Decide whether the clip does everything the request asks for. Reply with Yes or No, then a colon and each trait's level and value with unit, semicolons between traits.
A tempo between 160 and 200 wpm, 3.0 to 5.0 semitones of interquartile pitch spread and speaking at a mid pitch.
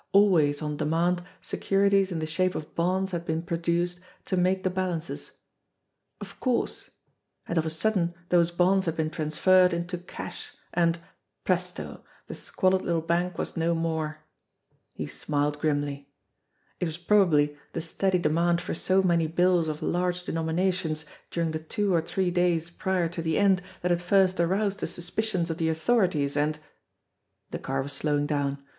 No: average, 165 wpm; narrow, 2.5 semitones; medium, 170 Hz